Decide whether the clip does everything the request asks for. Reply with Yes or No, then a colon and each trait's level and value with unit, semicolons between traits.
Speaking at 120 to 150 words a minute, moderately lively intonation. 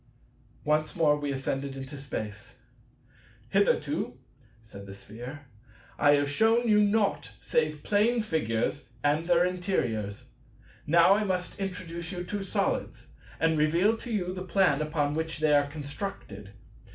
Yes: average, 140 wpm; average, 4.7 semitones